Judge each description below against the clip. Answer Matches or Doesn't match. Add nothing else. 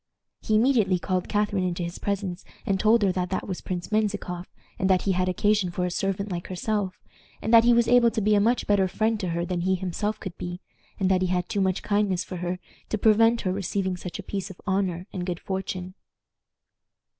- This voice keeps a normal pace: Doesn't match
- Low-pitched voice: Doesn't match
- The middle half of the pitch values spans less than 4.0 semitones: Matches